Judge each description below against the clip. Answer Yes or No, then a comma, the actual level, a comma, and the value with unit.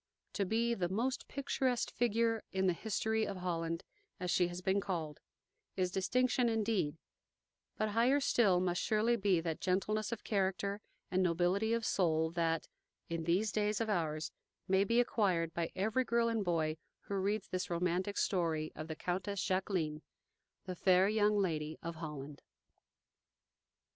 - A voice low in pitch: No, high, 190 Hz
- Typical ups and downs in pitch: Yes, average, 4.2 semitones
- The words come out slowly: No, average, 155 wpm